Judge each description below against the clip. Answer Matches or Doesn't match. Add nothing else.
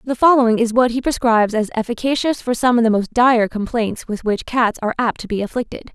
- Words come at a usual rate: Doesn't match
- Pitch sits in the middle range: Doesn't match